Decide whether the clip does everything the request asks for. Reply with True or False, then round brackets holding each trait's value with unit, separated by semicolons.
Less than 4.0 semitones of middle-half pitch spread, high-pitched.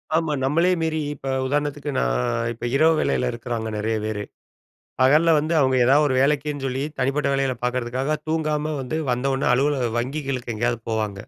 False (3.6 semitones; 135 Hz)